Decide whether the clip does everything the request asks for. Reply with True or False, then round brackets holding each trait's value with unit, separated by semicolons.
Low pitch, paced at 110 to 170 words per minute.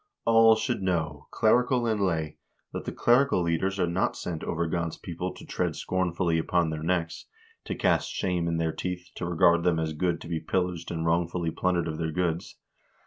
False (85 Hz; 195 wpm)